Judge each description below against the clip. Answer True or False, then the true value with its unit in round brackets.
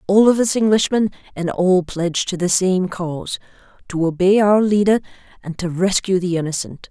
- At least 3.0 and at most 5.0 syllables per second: False (5.2 syllables/s)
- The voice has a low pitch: False (185 Hz)